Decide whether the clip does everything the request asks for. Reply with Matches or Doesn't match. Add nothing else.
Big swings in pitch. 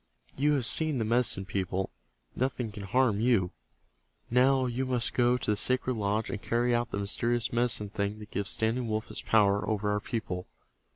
Doesn't match